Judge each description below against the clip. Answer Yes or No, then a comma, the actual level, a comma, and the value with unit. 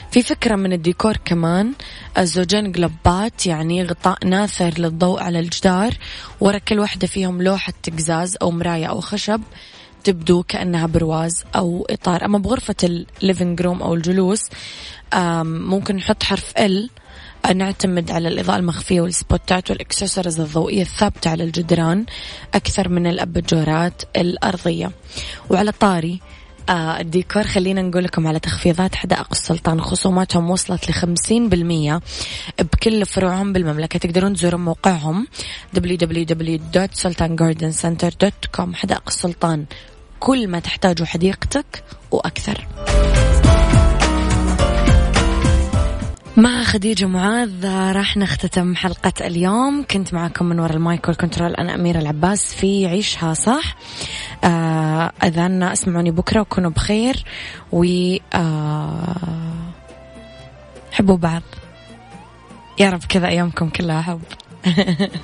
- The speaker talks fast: No, average, 105 wpm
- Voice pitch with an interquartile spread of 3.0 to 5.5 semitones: No, narrow, 2.5 semitones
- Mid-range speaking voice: Yes, medium, 180 Hz